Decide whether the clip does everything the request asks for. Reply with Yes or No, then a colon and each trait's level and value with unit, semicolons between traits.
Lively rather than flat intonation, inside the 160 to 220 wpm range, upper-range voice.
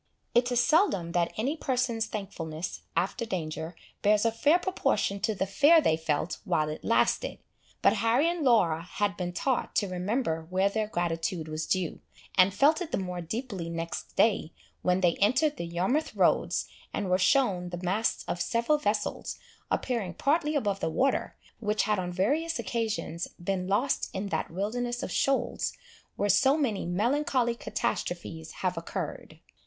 Yes: wide, 5.8 semitones; average, 165 wpm; high, 205 Hz